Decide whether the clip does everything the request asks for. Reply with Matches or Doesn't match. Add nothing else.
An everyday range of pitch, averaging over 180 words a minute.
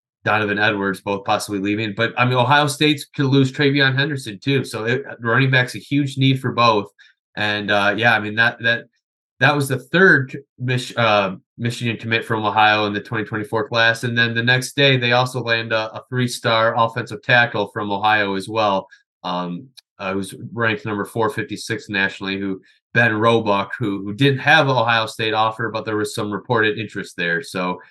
Matches